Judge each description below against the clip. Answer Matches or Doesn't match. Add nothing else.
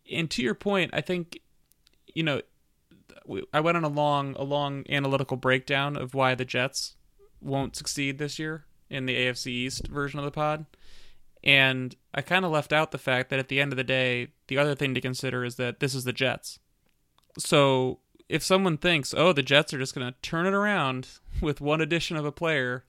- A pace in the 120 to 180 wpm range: Doesn't match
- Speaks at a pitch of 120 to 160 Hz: Matches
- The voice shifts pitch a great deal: Doesn't match